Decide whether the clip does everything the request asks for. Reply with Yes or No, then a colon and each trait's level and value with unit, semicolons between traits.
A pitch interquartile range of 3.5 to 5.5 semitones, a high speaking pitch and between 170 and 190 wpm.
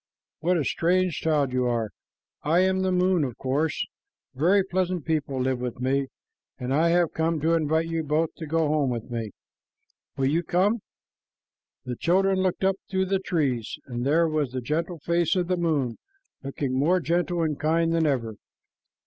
No: average, 4.5 semitones; medium, 160 Hz; average, 180 wpm